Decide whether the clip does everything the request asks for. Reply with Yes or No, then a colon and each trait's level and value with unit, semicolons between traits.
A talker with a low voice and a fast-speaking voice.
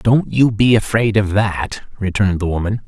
No: low, 105 Hz; average, 190 wpm